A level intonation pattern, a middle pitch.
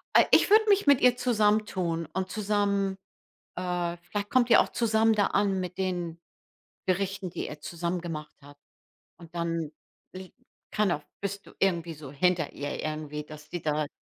No: average, 3.9 semitones; medium, 180 Hz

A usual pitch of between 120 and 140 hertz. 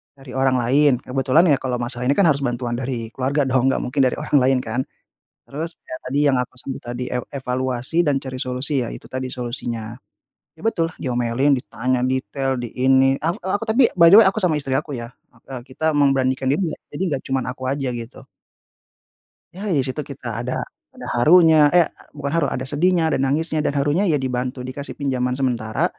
Yes: low, 135 Hz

